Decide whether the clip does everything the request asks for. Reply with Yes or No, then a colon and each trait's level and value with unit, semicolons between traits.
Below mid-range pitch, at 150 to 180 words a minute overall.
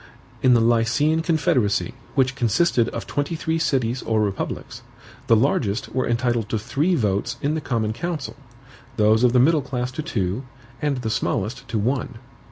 Yes: low, 125 Hz; average, 170 wpm